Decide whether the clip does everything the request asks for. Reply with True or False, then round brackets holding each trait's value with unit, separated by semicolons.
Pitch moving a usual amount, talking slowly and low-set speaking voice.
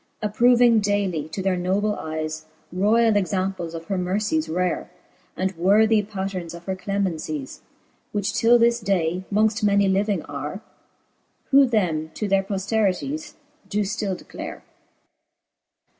False (3.0 semitones; 130 wpm; 195 Hz)